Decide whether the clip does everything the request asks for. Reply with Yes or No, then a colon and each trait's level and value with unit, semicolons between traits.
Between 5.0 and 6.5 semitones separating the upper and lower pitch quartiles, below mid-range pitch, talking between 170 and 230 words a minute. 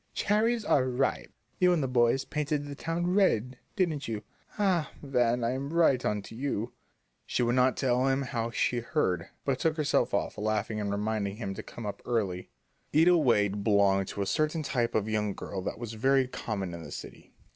Yes: wide, 5.4 semitones; low, 125 Hz; average, 195 wpm